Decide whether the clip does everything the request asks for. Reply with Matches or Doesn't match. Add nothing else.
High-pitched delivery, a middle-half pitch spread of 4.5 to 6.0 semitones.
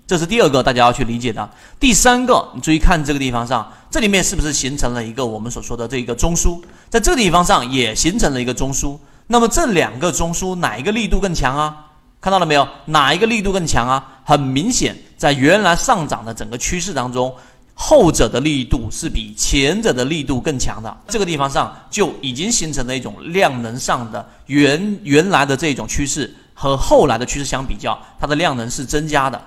Doesn't match